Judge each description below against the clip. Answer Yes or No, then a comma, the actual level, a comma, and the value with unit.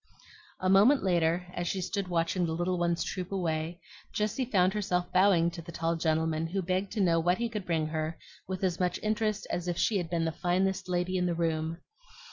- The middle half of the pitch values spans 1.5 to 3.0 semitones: Yes, narrow, 2.4 semitones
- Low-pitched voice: No, medium, 180 Hz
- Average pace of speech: No, fast, 215 wpm